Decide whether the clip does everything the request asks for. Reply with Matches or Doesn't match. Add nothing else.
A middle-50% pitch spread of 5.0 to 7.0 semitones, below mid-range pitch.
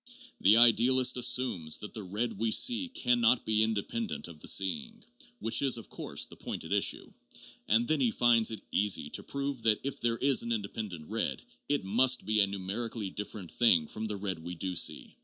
Doesn't match